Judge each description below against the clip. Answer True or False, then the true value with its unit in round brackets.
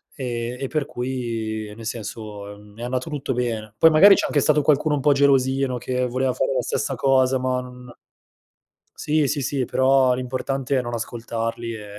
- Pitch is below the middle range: True (125 Hz)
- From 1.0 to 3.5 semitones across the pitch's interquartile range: True (2.6 semitones)